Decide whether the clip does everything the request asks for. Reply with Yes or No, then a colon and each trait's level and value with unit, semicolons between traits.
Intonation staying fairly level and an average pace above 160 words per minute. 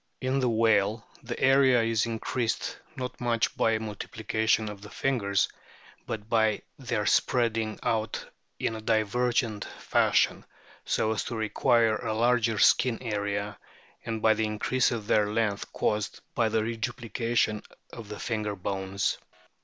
No: narrow, 1.8 semitones; average, 145 wpm